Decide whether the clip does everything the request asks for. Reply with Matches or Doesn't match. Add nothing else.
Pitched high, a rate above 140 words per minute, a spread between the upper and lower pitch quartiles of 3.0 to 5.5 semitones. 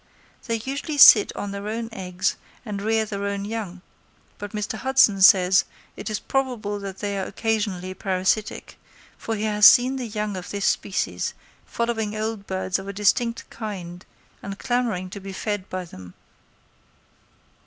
Doesn't match